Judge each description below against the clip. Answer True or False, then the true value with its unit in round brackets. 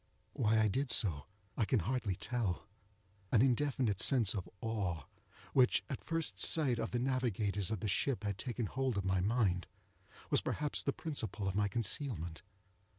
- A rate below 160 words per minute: False (165 wpm)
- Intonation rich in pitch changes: False (4.7 semitones)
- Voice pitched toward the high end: False (110 Hz)